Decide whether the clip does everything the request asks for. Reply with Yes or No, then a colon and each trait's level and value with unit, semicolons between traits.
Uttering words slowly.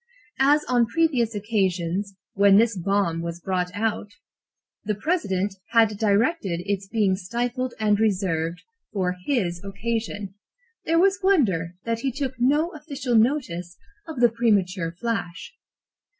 Yes: slow, 130 wpm